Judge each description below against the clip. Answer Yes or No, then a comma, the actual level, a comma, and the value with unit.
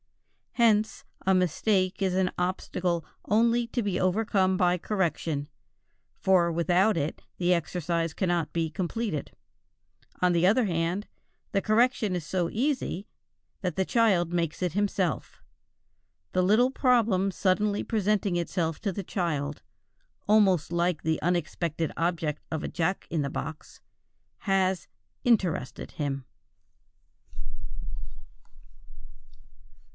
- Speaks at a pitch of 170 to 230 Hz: Yes, medium, 185 Hz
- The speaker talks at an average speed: No, slow, 115 wpm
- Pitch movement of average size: Yes, average, 3.4 semitones